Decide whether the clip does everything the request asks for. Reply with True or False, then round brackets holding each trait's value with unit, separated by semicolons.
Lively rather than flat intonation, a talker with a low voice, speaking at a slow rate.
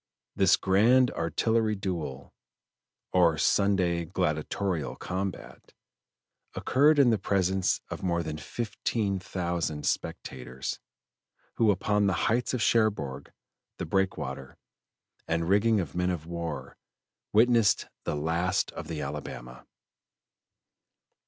False (4.1 semitones; 90 Hz; 105 wpm)